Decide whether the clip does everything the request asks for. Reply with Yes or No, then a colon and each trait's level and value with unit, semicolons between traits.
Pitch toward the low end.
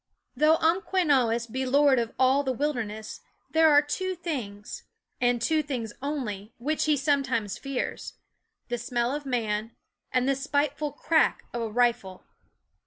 No: very high, 260 Hz